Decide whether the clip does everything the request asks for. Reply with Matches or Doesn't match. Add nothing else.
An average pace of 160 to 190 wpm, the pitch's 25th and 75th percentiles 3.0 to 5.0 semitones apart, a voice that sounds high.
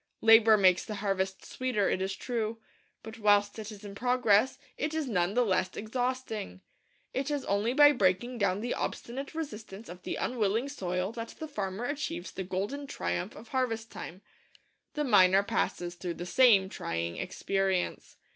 Matches